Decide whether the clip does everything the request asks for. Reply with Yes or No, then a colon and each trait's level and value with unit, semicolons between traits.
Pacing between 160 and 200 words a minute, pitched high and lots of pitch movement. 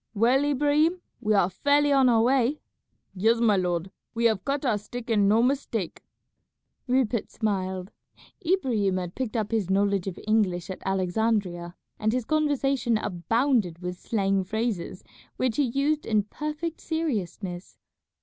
No: average, 145 wpm; high, 225 Hz; wide, 5.7 semitones